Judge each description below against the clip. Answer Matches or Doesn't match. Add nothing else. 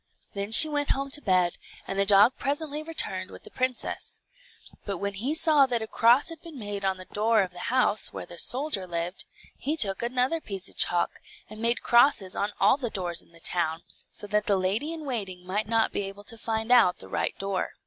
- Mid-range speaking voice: Doesn't match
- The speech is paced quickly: Matches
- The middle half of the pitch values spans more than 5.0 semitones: Matches